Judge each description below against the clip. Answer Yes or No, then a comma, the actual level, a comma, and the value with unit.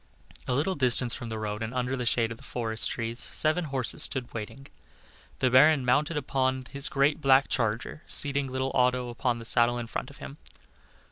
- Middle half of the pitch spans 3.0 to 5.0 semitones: No, narrow, 2.6 semitones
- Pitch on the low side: Yes, low, 125 Hz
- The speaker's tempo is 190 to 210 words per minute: Yes, average, 195 wpm